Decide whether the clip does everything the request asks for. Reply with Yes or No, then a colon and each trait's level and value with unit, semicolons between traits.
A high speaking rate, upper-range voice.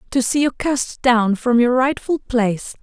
No: average, 190 wpm; very high, 250 Hz